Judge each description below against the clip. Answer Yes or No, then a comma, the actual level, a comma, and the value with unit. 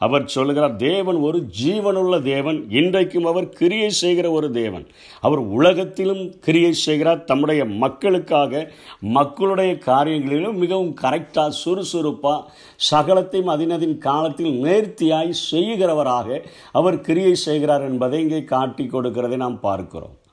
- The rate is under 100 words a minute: No, average, 110 wpm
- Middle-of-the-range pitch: Yes, medium, 155 Hz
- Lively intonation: No, average, 4.0 semitones